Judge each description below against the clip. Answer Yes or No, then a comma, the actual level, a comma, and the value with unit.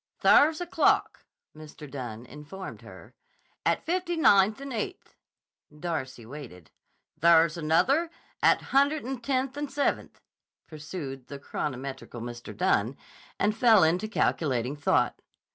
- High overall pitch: No, medium, 165 Hz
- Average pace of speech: No, slow, 125 wpm